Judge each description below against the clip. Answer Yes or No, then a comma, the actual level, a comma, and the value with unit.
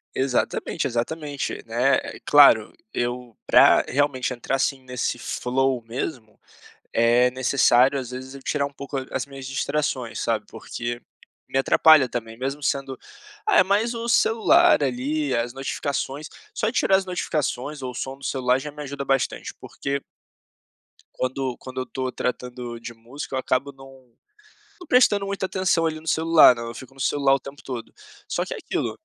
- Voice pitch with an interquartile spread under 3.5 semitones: Yes, average, 2.8 semitones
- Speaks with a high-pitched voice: No, low, 135 Hz